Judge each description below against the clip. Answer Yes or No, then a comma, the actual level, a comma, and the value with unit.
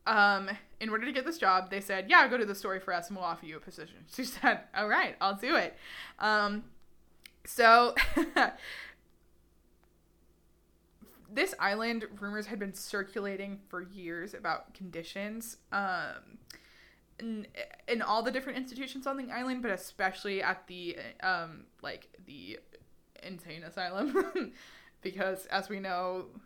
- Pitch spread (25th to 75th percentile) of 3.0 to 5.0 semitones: Yes, average, 4.2 semitones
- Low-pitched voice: No, high, 205 Hz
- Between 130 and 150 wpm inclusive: Yes, average, 145 wpm